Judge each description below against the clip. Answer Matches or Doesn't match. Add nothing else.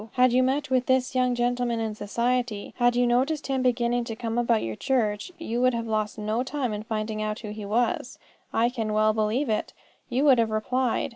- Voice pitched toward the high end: Matches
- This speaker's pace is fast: Matches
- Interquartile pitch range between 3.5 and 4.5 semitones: Doesn't match